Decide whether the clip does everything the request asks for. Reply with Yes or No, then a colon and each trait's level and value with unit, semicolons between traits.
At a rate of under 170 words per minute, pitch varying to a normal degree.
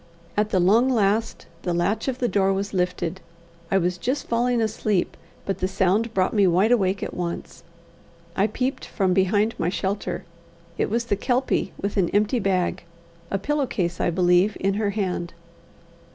No: average, 175 wpm; average, 3.3 semitones